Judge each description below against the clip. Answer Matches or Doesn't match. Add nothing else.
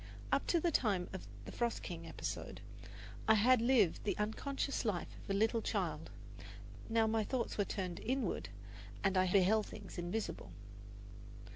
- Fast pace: Doesn't match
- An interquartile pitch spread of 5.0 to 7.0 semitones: Doesn't match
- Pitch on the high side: Matches